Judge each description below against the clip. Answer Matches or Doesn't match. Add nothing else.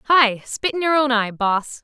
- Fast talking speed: Matches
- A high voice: Matches